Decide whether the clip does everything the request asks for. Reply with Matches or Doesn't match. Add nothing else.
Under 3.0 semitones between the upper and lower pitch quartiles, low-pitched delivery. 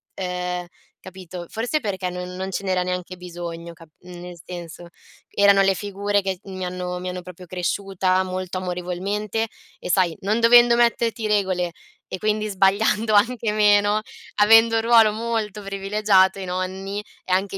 Doesn't match